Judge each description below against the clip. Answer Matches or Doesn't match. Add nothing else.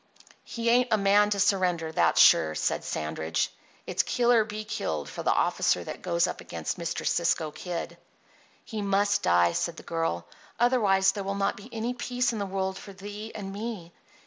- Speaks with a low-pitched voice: Doesn't match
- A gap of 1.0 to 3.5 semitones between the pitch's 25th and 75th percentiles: Doesn't match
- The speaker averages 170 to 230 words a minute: Matches